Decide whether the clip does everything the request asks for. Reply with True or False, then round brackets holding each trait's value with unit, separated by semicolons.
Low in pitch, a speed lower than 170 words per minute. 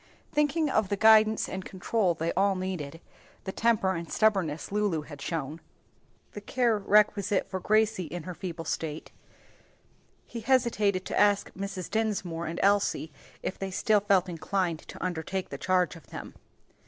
False (190 Hz; 160 wpm)